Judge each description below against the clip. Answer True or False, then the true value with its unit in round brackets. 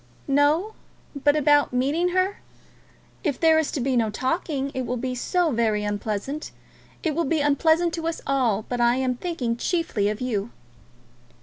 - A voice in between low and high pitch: False (275 Hz)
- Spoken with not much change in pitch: False (5.1 semitones)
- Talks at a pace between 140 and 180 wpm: True (170 wpm)